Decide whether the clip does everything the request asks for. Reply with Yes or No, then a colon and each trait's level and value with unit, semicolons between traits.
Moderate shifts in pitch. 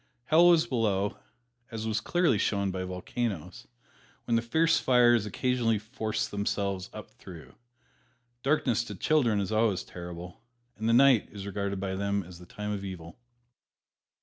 Yes: average, 3.6 semitones